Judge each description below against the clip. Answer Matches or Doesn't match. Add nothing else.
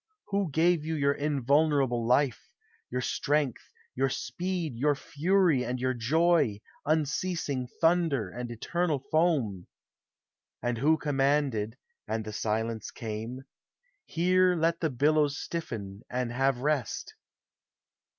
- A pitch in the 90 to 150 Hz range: Matches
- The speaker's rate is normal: Doesn't match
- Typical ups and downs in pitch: Matches